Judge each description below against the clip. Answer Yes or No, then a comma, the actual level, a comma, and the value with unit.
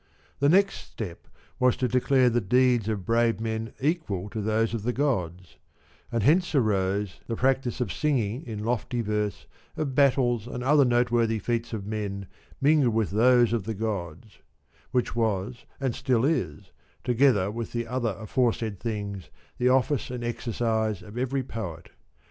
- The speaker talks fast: No, average, 160 wpm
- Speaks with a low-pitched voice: Yes, low, 115 Hz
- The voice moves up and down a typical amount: Yes, average, 3.1 semitones